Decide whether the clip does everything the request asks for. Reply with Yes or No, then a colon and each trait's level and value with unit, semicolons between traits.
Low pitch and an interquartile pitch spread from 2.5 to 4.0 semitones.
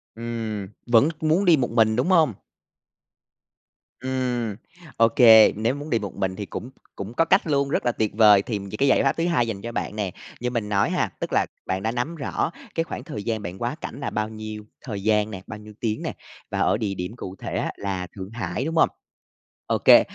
Yes: low, 115 Hz; average, 3.7 semitones